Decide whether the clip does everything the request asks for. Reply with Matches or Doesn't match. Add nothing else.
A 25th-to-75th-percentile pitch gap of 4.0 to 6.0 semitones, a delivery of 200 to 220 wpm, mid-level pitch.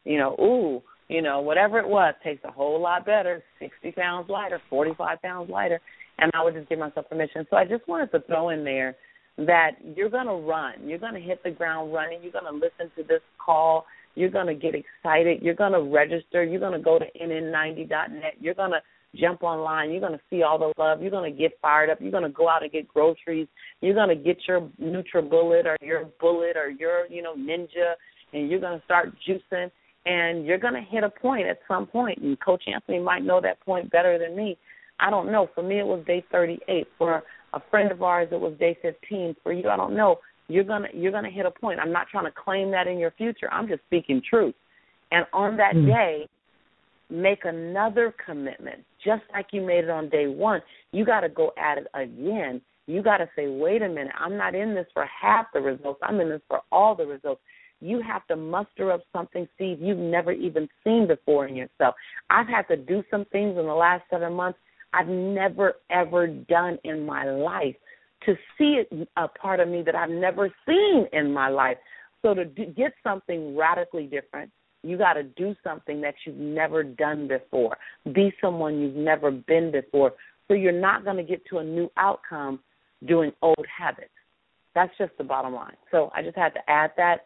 Doesn't match